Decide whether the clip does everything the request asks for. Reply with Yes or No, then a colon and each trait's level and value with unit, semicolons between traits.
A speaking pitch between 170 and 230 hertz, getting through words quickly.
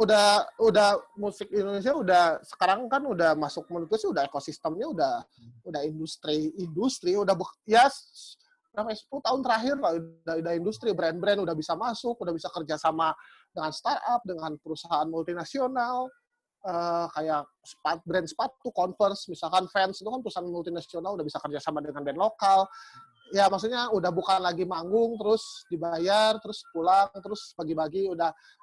Yes: high, 190 Hz; fast, 150 wpm